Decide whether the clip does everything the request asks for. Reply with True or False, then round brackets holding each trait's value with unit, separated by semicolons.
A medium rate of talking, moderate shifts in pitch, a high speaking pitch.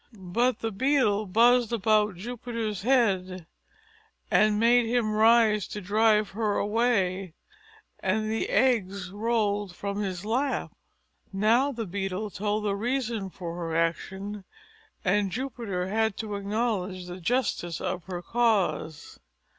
False (125 wpm; 3.4 semitones; 210 Hz)